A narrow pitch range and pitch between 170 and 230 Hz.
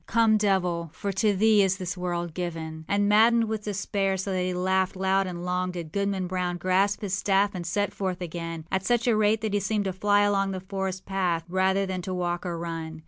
Yes: narrow, 2.2 semitones; high, 190 Hz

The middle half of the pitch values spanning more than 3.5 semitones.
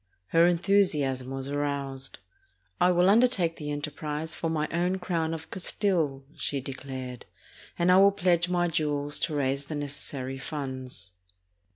Yes: average, 4.1 semitones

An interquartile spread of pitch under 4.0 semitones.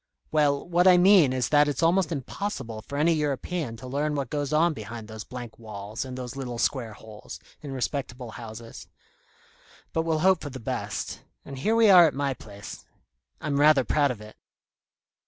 No: average, 4.8 semitones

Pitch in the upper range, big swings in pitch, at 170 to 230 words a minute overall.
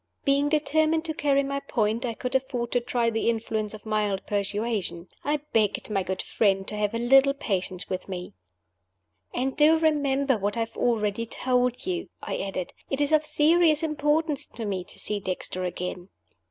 Yes: high, 235 Hz; wide, 5.7 semitones; average, 180 wpm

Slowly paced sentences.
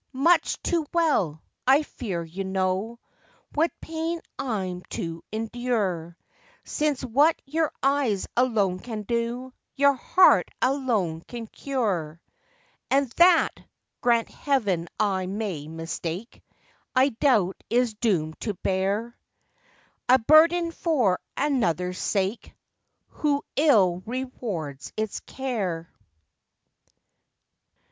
Yes: slow, 100 wpm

